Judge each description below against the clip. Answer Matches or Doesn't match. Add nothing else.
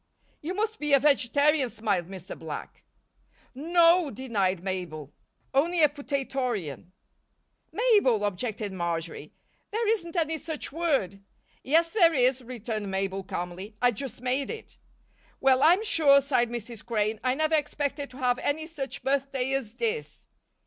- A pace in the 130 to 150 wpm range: Matches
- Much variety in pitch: Matches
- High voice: Matches